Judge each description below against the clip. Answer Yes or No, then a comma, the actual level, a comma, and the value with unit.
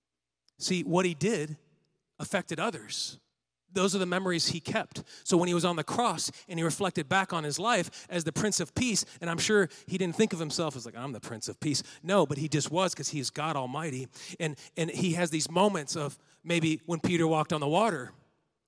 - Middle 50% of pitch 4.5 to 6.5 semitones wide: No, average, 3.8 semitones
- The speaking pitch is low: No, medium, 165 Hz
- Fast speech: Yes, fast, 225 wpm